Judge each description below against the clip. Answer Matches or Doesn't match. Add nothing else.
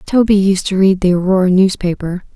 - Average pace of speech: Matches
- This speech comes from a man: Doesn't match